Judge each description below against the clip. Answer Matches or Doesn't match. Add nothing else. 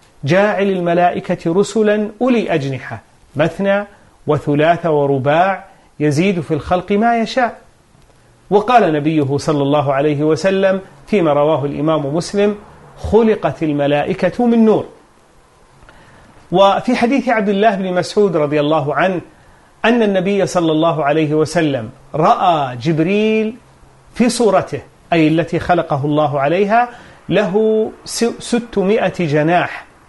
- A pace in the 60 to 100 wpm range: Doesn't match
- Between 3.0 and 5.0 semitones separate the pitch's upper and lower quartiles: Doesn't match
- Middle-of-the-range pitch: Matches